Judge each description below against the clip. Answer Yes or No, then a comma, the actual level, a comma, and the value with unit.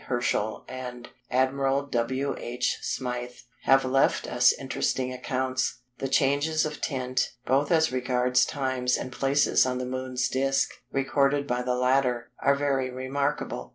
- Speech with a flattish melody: Yes, narrow, 1.5 semitones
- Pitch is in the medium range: No, low, 130 Hz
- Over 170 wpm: No, average, 140 wpm